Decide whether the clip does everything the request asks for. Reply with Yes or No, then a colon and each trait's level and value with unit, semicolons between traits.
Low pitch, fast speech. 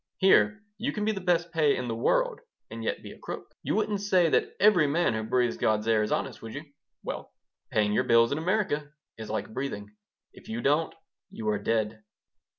No: medium, 145 Hz; fast, 210 wpm